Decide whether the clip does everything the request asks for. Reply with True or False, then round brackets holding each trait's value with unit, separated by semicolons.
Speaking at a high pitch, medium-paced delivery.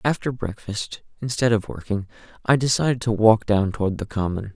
False (110 Hz; 170 wpm)